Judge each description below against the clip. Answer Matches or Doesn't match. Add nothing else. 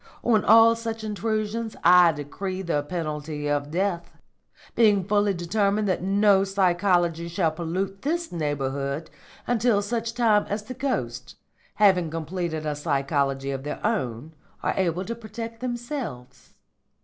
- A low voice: Doesn't match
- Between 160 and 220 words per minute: Doesn't match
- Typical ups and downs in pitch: Doesn't match